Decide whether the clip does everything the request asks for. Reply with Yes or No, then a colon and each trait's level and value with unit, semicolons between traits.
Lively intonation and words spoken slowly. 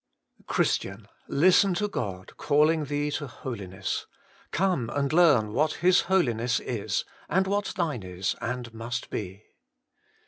Yes: wide, 7.4 semitones; slow, 130 wpm